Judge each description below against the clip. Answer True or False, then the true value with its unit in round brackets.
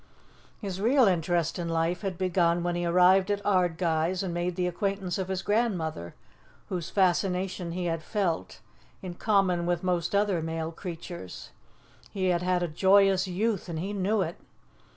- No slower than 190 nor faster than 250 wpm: False (165 wpm)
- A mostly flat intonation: True (2.2 semitones)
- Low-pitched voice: False (180 Hz)